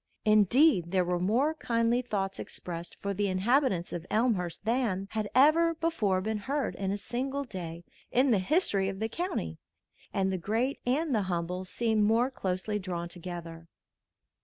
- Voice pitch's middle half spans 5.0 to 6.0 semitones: Yes, wide, 5.4 semitones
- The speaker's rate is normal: Yes, average, 160 wpm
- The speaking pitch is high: Yes, high, 205 Hz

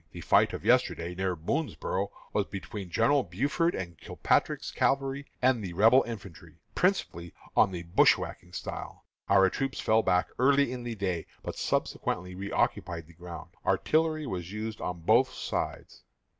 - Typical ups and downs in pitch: No, wide, 6.5 semitones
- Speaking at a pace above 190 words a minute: No, average, 145 wpm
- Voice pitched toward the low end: Yes, low, 100 Hz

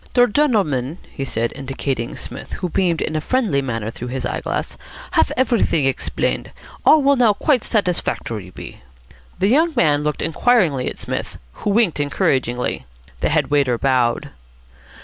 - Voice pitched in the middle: Yes, medium, 150 Hz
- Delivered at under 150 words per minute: No, average, 155 wpm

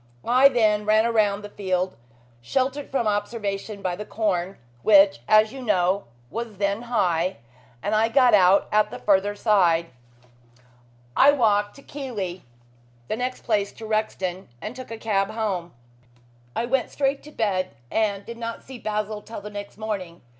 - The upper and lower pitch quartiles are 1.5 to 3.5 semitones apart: Yes, average, 2.8 semitones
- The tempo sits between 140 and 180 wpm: Yes, average, 160 wpm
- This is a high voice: Yes, high, 210 Hz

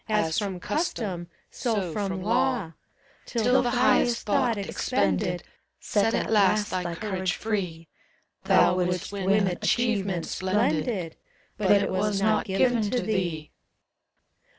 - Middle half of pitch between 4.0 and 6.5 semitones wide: No, average, 3.5 semitones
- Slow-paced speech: Yes, slow, 125 wpm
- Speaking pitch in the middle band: No, high, 200 Hz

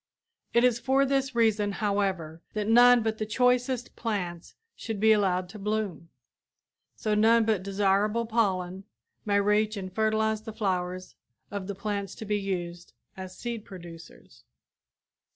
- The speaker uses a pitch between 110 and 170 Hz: No, high, 210 Hz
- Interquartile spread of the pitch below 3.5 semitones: Yes, average, 2.8 semitones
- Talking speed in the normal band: Yes, average, 145 wpm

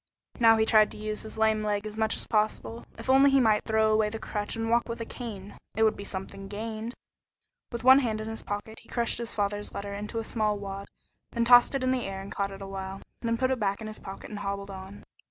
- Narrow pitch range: Yes, narrow, 2.2 semitones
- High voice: Yes, high, 215 Hz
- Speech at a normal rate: No, fast, 255 wpm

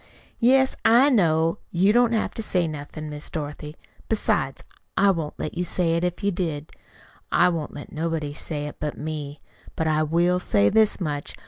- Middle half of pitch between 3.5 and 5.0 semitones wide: Yes, average, 4.0 semitones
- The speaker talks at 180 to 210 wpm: Yes, average, 185 wpm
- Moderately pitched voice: Yes, medium, 165 Hz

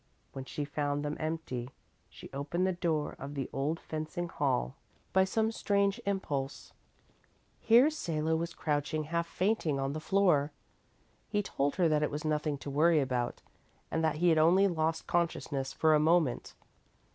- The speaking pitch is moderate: Yes, medium, 155 Hz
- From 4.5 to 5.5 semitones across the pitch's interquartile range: No, average, 3.1 semitones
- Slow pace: No, average, 165 wpm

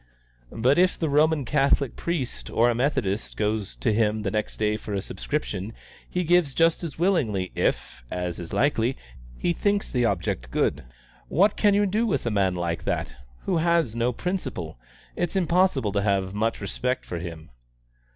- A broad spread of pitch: Yes, wide, 8.7 semitones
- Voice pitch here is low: Yes, low, 120 Hz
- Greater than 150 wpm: Yes, average, 175 wpm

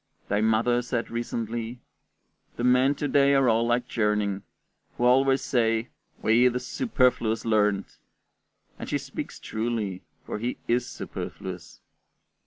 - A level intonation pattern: Yes, narrow, 2.3 semitones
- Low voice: Yes, low, 120 Hz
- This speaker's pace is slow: Yes, slow, 130 wpm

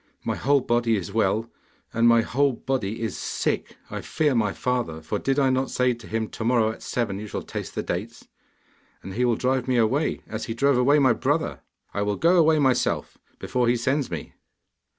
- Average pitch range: Yes, average, 3.2 semitones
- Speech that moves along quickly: Yes, fast, 210 wpm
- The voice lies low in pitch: Yes, low, 120 Hz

